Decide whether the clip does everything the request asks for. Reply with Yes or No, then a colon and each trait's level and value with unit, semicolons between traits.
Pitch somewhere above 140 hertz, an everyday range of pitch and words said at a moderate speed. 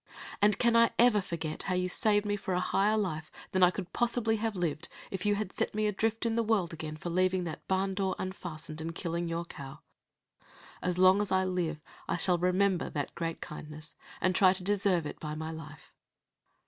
No: medium, 185 Hz; average, 3.7 semitones; fast, 210 wpm